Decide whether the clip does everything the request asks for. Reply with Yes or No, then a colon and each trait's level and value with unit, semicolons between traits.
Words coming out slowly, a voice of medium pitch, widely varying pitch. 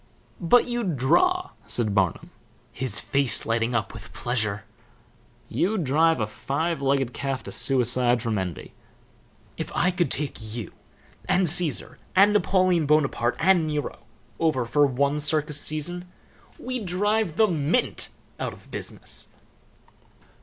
Yes: slow, 130 wpm; medium, 150 Hz; wide, 6.5 semitones